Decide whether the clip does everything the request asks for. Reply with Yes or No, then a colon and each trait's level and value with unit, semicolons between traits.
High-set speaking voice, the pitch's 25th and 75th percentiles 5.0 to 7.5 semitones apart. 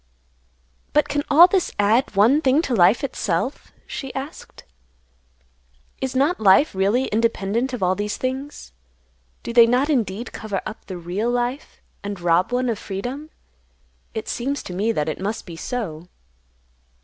Yes: high, 230 Hz; average, 5.3 semitones